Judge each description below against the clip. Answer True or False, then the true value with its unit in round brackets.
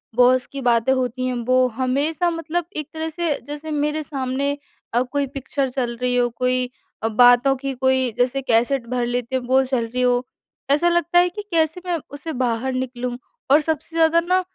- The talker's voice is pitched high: True (265 Hz)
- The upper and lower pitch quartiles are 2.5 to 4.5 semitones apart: True (3.7 semitones)